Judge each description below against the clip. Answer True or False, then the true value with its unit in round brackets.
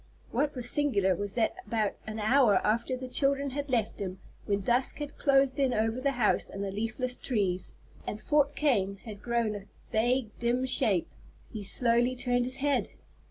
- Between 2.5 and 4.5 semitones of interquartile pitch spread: True (3.9 semitones)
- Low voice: False (240 Hz)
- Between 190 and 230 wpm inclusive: False (180 wpm)